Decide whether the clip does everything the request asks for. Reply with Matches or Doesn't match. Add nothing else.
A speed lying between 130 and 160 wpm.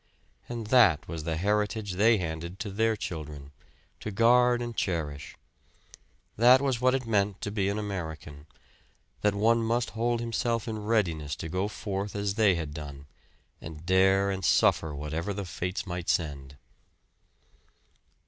Matches